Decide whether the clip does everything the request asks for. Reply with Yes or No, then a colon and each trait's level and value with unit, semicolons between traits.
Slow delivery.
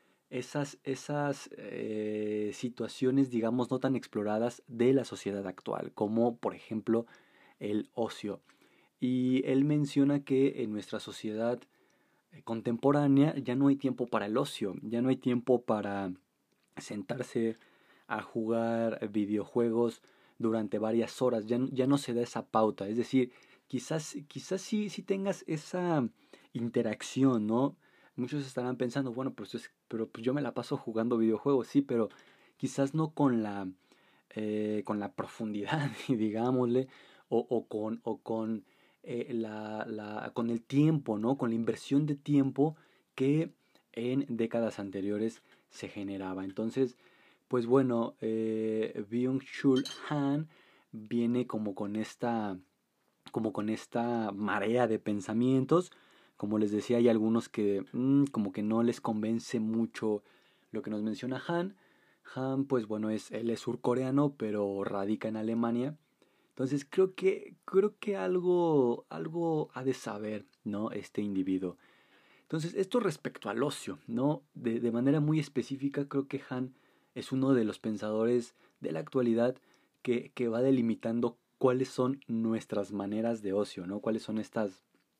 No: average, 140 wpm